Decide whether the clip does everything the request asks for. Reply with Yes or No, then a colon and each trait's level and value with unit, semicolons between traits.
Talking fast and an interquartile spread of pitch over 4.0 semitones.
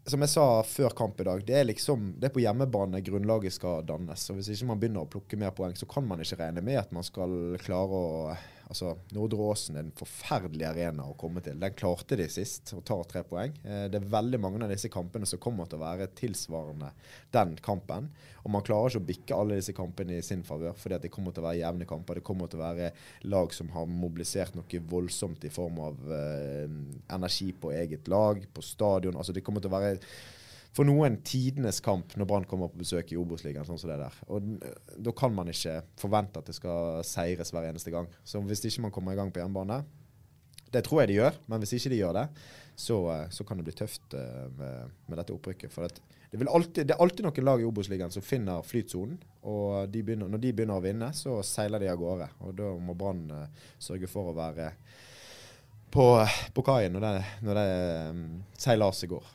Yes: fast, 215 wpm; average, 4.5 semitones